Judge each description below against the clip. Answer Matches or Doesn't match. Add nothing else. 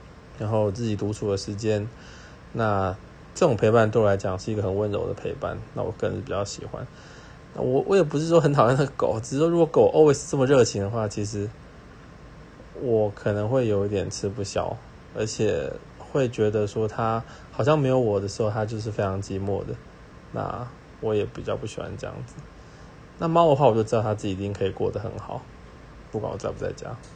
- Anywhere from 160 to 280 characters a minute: Doesn't match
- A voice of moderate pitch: Doesn't match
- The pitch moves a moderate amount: Matches